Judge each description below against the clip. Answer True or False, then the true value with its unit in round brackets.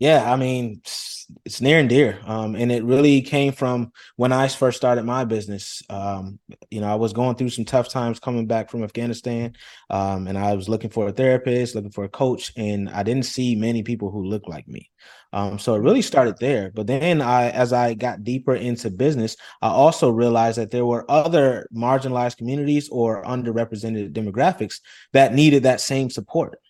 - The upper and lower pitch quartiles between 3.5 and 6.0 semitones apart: False (2.8 semitones)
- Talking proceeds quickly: False (195 wpm)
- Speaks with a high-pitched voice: False (120 Hz)